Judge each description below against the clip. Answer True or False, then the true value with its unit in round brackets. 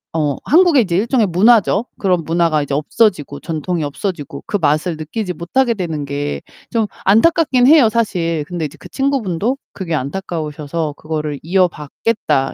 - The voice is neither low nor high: True (175 Hz)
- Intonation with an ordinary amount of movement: False (6.5 semitones)